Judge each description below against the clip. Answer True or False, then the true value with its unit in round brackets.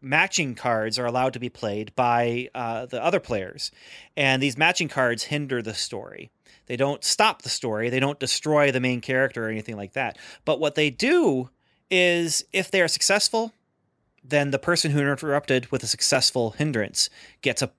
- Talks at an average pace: True (180 wpm)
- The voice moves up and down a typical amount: True (3.7 semitones)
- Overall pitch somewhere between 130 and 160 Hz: True (135 Hz)